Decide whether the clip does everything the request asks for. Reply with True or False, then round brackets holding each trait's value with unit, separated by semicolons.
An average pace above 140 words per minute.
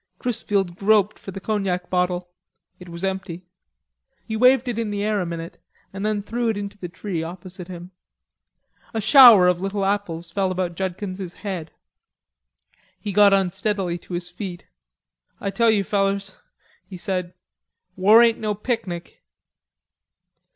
True (150 wpm)